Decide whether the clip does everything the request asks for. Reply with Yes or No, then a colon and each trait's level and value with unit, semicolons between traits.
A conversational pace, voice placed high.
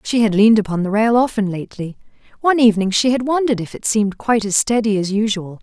No: fast, 225 wpm; high, 215 Hz